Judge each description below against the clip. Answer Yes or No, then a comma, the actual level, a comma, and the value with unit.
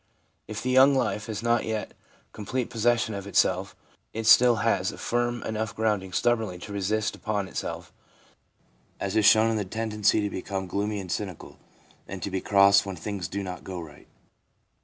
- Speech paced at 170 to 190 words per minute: Yes, average, 175 wpm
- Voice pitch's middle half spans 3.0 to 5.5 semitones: No, narrow, 2.5 semitones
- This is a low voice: Yes, low, 105 Hz